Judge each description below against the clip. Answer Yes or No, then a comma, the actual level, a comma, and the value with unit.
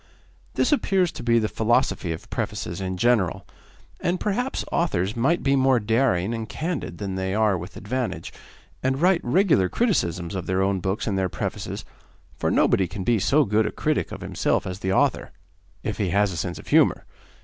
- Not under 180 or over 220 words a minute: Yes, average, 190 wpm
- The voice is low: Yes, low, 105 Hz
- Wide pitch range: Yes, wide, 6.0 semitones